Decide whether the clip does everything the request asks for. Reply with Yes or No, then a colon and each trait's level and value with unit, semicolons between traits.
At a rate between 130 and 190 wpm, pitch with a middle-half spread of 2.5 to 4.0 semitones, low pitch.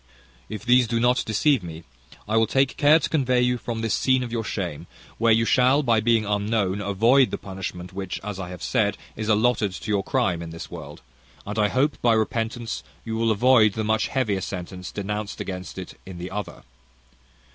No: average, 200 wpm; average, 3.7 semitones; low, 110 Hz